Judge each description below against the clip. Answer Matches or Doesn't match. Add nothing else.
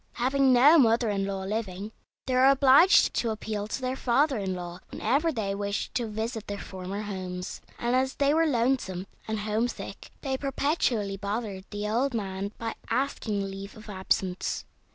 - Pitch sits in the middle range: Doesn't match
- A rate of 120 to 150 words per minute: Doesn't match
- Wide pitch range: Doesn't match